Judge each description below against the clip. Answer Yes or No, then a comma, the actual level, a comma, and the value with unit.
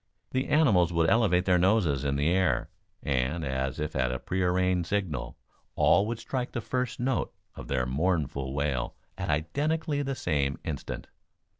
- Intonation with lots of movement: Yes, wide, 8.1 semitones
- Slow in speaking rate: No, average, 160 wpm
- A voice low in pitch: Yes, very low, 90 Hz